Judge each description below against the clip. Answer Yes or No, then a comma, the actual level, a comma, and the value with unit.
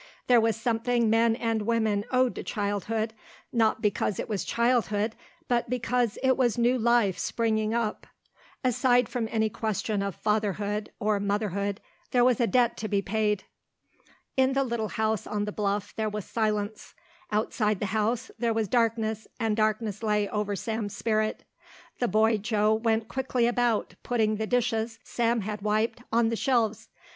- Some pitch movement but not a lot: No, narrow, 2.0 semitones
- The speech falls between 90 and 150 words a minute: No, average, 165 wpm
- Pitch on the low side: No, high, 220 Hz